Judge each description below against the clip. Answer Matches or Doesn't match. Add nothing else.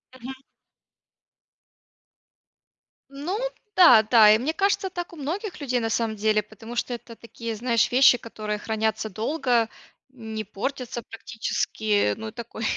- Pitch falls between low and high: Doesn't match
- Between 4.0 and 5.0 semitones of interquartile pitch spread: Doesn't match